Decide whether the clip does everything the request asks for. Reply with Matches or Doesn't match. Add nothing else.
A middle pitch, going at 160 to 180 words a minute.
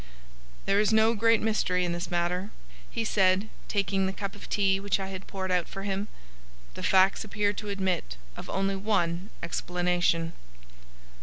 Doesn't match